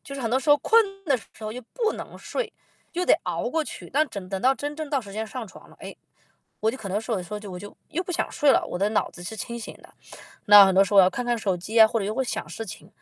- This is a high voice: Yes, high, 225 Hz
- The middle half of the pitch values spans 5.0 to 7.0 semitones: Yes, wide, 5.6 semitones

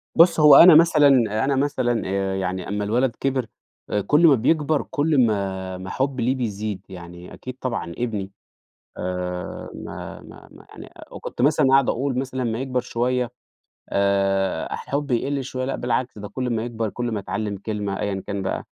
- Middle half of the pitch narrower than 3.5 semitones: No, average, 5.3 semitones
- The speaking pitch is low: Yes, low, 120 Hz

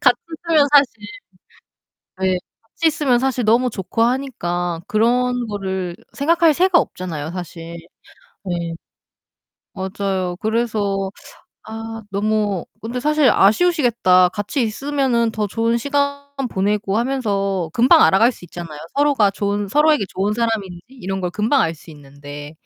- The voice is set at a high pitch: Yes, high, 215 Hz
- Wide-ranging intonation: No, average, 5.0 semitones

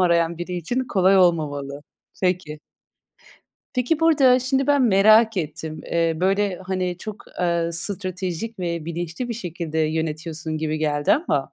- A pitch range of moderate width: Yes, average, 4.7 semitones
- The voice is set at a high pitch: No, medium, 175 Hz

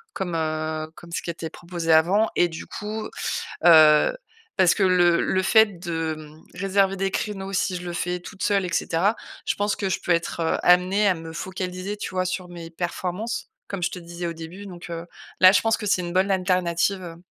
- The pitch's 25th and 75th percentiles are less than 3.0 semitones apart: Yes, narrow, 2.4 semitones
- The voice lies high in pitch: No, medium, 180 Hz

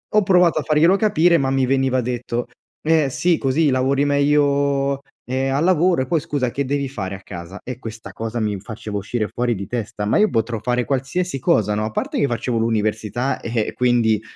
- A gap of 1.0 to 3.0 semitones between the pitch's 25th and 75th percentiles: No, average, 4.2 semitones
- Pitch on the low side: Yes, low, 130 Hz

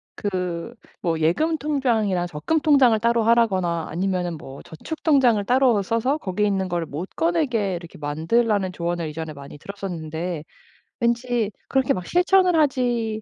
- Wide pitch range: Yes, wide, 6.3 semitones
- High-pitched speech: Yes, high, 205 Hz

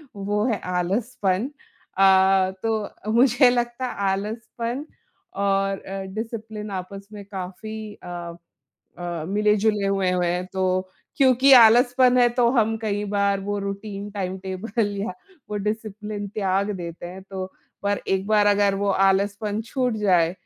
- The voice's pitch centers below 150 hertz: No, high, 205 Hz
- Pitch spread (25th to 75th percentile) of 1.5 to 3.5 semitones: Yes, narrow, 2.4 semitones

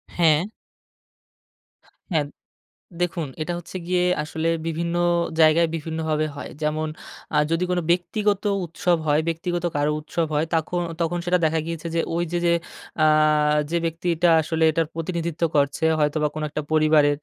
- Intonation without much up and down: Yes, narrow, 1.8 semitones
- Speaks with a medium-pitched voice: Yes, medium, 165 Hz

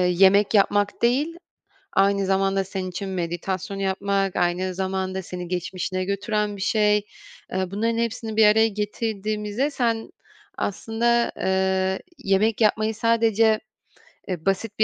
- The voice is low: No, high, 200 Hz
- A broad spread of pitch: No, narrow, 2.6 semitones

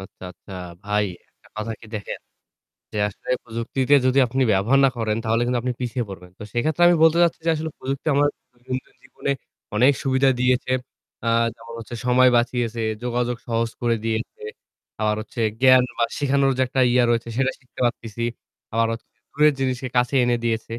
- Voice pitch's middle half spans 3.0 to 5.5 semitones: No, narrow, 2.5 semitones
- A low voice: Yes, low, 120 Hz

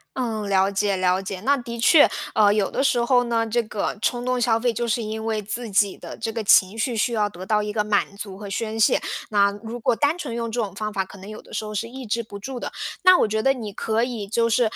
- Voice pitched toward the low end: No, high, 220 Hz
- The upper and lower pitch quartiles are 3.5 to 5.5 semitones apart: No, narrow, 2.6 semitones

